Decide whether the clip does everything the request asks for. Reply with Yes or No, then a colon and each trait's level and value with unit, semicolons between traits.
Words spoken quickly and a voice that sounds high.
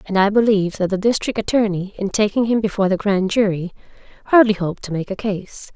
Yes: fast, 210 wpm; high, 200 Hz